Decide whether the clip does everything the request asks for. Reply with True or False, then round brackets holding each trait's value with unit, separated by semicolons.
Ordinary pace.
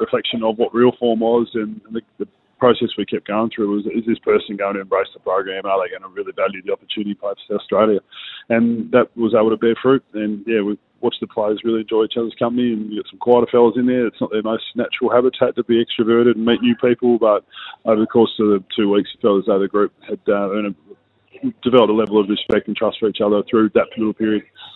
False (250 wpm)